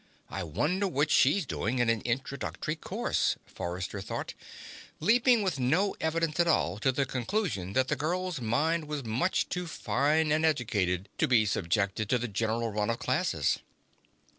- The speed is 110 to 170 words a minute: Yes, average, 165 wpm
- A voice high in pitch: No, low, 130 Hz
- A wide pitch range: Yes, wide, 6.7 semitones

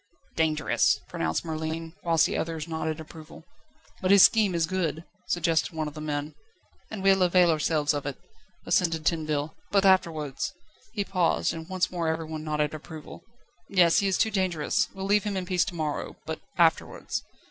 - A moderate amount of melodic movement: Yes, average, 3.0 semitones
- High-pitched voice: No, medium, 165 Hz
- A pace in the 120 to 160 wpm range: No, average, 170 wpm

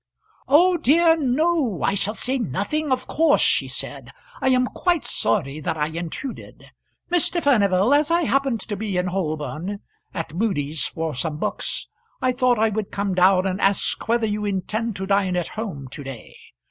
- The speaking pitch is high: Yes, high, 205 Hz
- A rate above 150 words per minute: Yes, average, 175 wpm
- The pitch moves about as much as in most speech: No, wide, 6.5 semitones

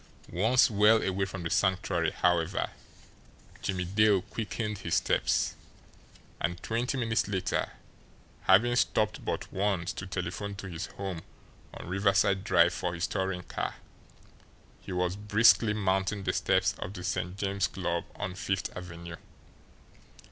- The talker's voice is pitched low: Yes, very low, 95 Hz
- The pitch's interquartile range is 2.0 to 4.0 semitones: Yes, narrow, 2.5 semitones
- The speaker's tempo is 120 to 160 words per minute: Yes, slow, 135 wpm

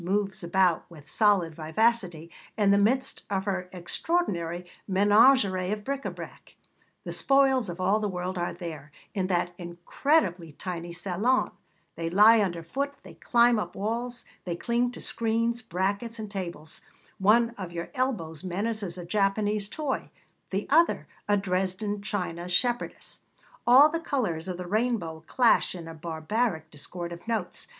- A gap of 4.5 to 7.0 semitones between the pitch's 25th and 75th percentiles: Yes, average, 4.9 semitones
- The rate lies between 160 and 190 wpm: No, average, 150 wpm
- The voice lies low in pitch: No, high, 195 Hz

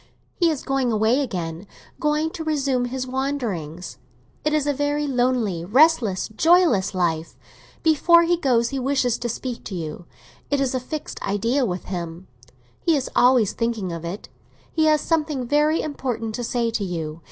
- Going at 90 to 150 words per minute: No, average, 165 wpm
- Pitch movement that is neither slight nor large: No, wide, 7.3 semitones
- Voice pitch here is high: Yes, high, 245 Hz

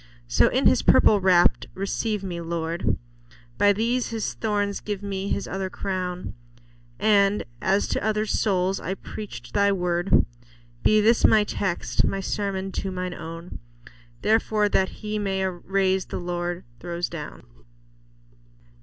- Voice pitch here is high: Yes, high, 195 Hz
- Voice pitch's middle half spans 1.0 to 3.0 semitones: Yes, narrow, 2.5 semitones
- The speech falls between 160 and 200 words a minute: No, average, 140 wpm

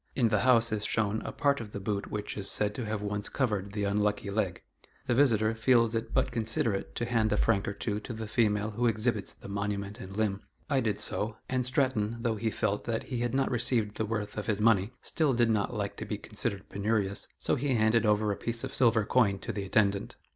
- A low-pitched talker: Yes, low, 110 Hz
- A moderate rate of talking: No, fast, 235 wpm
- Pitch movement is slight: Yes, narrow, 2.3 semitones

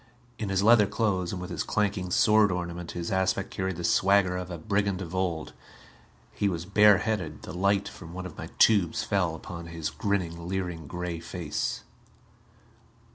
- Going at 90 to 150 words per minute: No, average, 175 wpm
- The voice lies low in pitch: Yes, very low, 90 Hz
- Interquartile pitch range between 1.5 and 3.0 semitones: Yes, narrow, 2.6 semitones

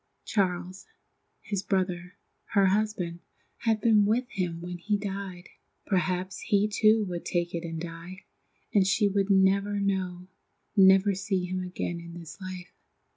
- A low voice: No, high, 190 Hz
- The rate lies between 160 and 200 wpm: No, average, 145 wpm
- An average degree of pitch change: No, narrow, 2.2 semitones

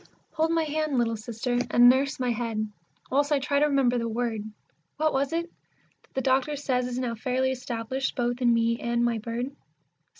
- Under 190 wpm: No, average, 195 wpm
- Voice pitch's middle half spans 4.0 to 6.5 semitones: No, average, 2.8 semitones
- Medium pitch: No, very high, 250 Hz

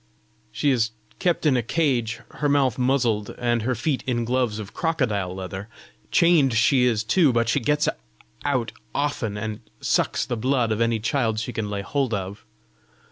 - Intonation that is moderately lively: Yes, average, 4.1 semitones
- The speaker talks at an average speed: Yes, average, 175 wpm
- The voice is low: Yes, low, 120 Hz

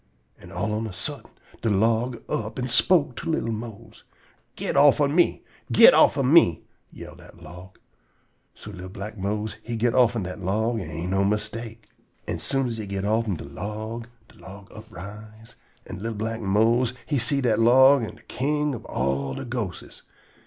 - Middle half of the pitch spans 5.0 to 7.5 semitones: No, average, 3.5 semitones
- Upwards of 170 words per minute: Yes, average, 180 wpm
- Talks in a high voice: No, low, 110 Hz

